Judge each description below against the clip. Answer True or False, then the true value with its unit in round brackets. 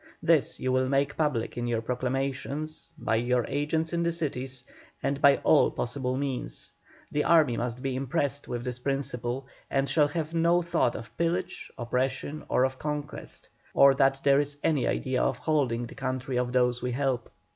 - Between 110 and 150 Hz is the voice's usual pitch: True (135 Hz)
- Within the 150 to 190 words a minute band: True (180 wpm)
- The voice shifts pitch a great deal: False (2.8 semitones)